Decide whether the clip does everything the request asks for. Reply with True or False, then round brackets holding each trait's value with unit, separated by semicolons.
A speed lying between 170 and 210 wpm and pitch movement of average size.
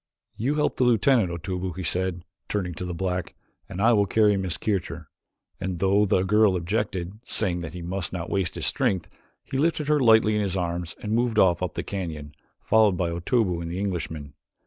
True (200 wpm; 3.6 semitones)